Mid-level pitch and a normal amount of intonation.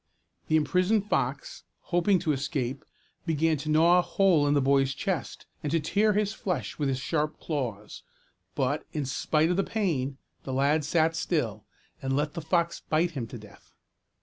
Yes: medium, 155 Hz; average, 4.2 semitones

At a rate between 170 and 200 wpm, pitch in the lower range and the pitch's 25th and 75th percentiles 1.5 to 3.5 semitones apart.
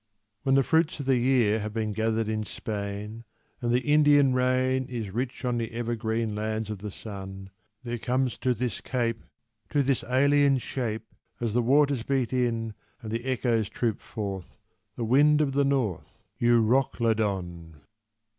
No: average, 160 wpm; low, 120 Hz; average, 3.1 semitones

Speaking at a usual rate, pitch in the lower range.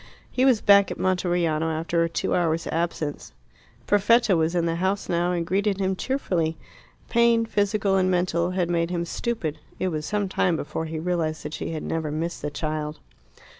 No: average, 185 wpm; medium, 175 Hz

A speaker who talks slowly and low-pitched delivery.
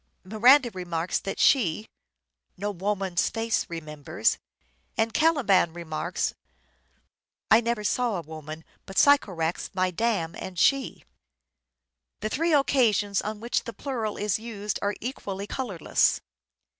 No: slow, 130 wpm; high, 205 Hz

